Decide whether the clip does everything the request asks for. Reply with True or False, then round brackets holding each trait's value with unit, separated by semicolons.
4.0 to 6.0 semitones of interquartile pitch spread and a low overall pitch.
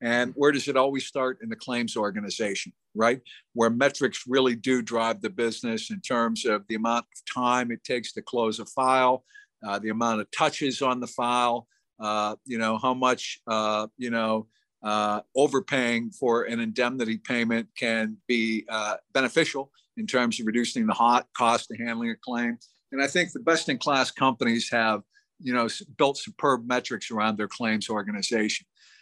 False (2.7 semitones; 120 Hz)